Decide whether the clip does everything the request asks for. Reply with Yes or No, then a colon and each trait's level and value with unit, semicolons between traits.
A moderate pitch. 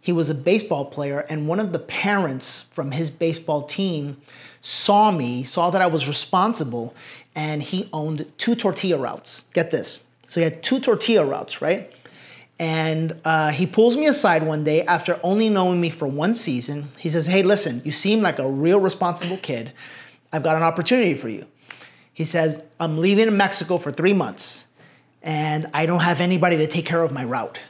Yes: medium, 165 Hz